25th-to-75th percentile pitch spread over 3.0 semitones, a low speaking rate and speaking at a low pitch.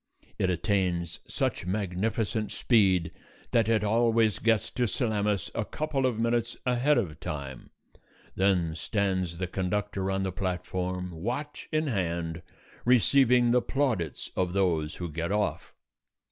Yes: average, 4.5 semitones; slow, 130 wpm; low, 100 Hz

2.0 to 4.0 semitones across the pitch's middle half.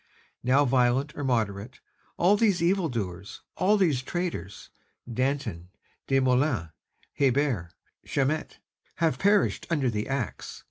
No: average, 5.3 semitones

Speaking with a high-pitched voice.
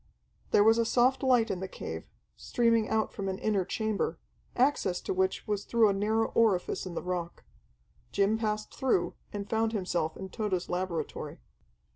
Yes: high, 210 Hz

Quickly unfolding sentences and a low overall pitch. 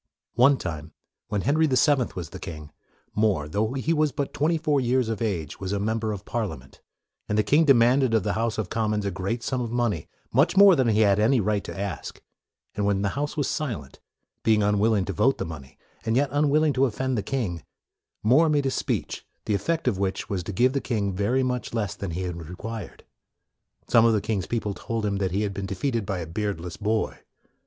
Yes: fast, 230 wpm; low, 110 Hz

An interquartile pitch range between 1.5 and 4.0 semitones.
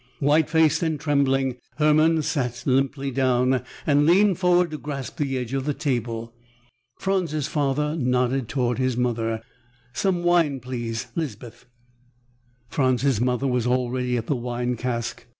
Yes: average, 3.5 semitones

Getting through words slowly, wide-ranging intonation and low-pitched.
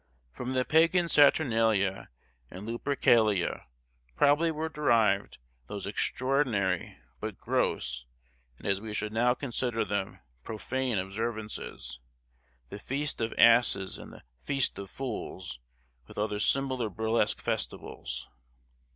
No: slow, 115 wpm; average, 4.7 semitones; low, 115 Hz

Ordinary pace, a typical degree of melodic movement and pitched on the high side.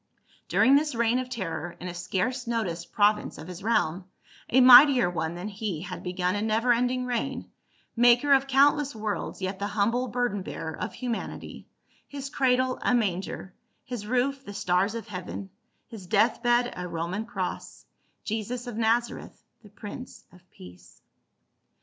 Yes: average, 160 wpm; average, 5.0 semitones; high, 220 Hz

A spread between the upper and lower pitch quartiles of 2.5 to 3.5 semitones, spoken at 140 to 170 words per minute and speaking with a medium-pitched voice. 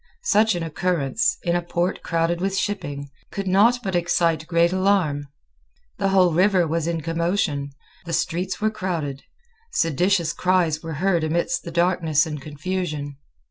Yes: average, 3.0 semitones; average, 150 wpm; medium, 170 Hz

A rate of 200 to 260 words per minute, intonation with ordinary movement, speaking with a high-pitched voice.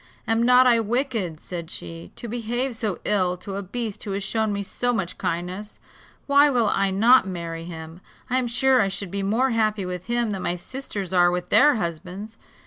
Yes: fast, 205 wpm; average, 4.8 semitones; high, 205 Hz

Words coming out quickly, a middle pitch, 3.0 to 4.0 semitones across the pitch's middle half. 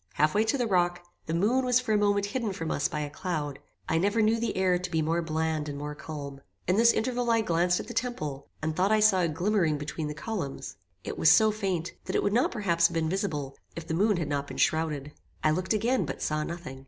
No: fast, 250 wpm; medium, 175 Hz; wide, 5.5 semitones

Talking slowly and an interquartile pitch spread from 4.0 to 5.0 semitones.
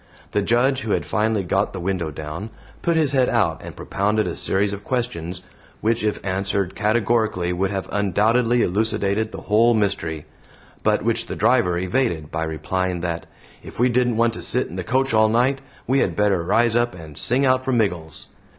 No: average, 190 wpm; average, 4.6 semitones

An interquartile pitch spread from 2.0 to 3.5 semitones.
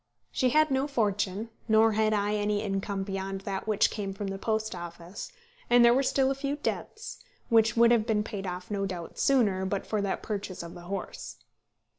Yes: average, 3.0 semitones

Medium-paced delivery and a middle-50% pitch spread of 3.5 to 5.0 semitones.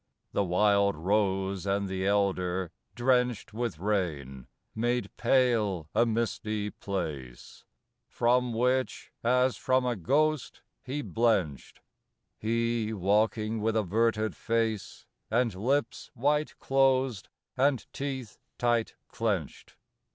No: slow, 105 wpm; average, 4.0 semitones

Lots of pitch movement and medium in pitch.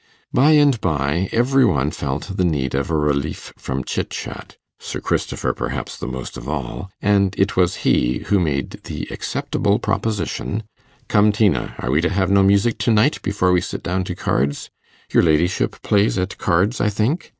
No: wide, 5.7 semitones; very low, 95 Hz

